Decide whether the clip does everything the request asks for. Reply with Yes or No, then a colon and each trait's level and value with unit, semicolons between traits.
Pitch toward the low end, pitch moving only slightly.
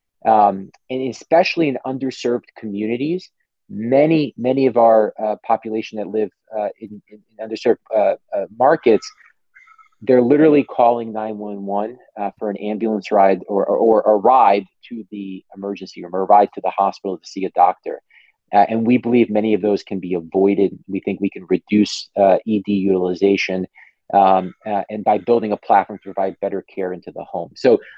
No: low, 105 Hz; average, 3.2 semitones